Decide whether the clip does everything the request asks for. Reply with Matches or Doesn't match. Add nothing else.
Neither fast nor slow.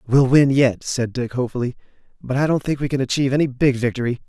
Doesn't match